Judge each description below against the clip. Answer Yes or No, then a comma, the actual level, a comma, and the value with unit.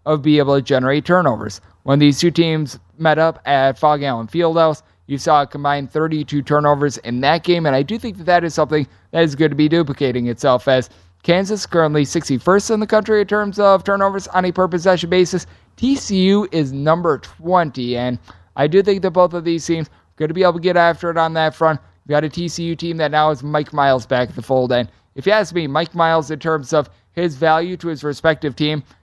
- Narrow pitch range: No, average, 3.7 semitones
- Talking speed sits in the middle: No, fast, 230 wpm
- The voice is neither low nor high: Yes, medium, 155 Hz